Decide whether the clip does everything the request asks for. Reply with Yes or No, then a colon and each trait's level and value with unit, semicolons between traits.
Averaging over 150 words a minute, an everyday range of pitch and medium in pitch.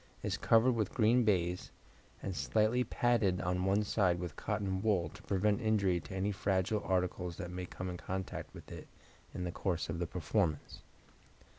No: average, 175 wpm; average, 3.0 semitones; very low, 95 Hz